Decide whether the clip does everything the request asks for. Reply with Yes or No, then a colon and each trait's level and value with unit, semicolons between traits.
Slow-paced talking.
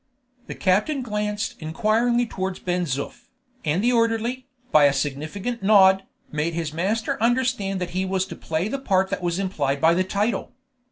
No: average, 170 wpm